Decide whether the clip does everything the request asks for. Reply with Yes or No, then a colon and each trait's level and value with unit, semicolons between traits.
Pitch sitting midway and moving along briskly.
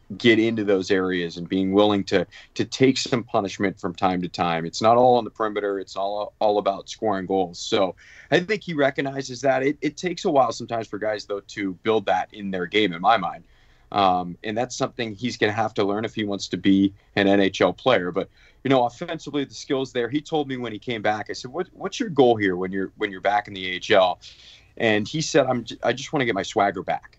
No: low, 110 Hz; fast, 245 wpm